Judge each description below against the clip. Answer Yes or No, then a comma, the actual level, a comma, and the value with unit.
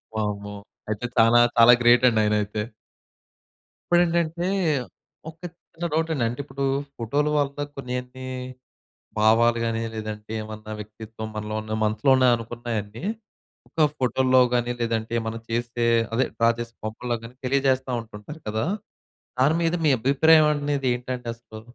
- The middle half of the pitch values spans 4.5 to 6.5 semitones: No, average, 3.7 semitones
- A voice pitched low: Yes, low, 120 Hz